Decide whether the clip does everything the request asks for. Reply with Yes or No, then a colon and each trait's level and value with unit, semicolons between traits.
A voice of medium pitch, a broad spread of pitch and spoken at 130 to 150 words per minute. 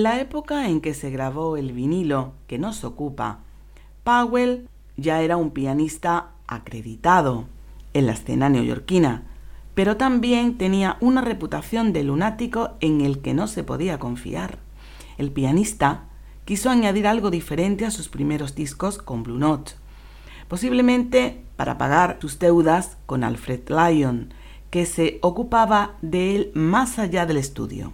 Yes: medium, 165 Hz; wide, 7.1 semitones; average, 140 wpm